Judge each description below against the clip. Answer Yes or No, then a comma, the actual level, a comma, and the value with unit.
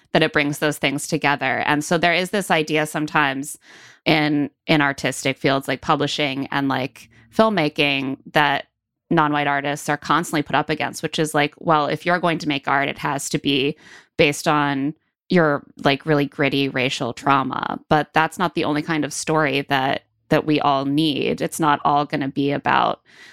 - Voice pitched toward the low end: No, medium, 150 Hz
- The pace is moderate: Yes, average, 185 wpm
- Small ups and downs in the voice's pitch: Yes, narrow, 2.1 semitones